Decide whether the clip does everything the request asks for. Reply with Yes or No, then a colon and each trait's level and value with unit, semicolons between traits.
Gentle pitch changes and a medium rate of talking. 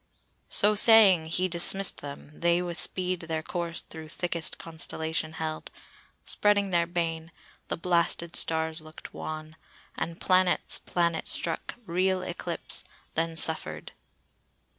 No: narrow, 2.1 semitones; slow, 120 wpm